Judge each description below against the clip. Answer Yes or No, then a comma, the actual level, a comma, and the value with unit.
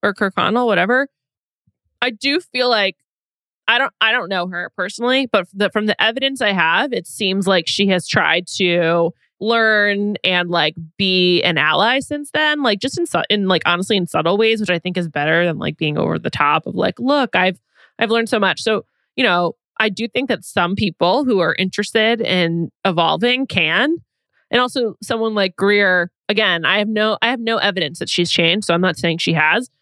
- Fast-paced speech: Yes, fast, 210 wpm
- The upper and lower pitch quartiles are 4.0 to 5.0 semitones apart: Yes, average, 4.7 semitones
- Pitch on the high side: Yes, high, 205 Hz